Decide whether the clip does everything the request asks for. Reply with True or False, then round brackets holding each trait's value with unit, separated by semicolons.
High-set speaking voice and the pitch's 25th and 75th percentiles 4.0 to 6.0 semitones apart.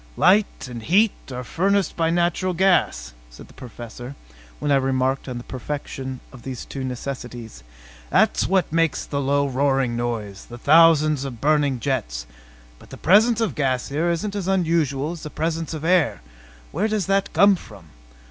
False (140 Hz; 5.4 semitones)